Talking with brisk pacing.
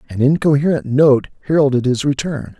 No: average, 140 wpm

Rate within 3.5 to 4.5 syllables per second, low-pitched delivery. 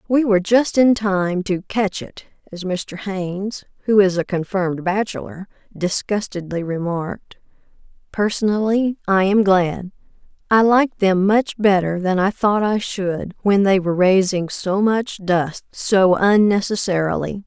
No: 4.2 syllables/s; high, 195 Hz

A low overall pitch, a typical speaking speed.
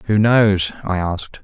Yes: low, 100 Hz; average, 165 wpm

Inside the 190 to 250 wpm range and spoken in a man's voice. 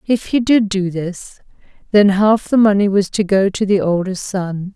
No: average, 200 wpm; female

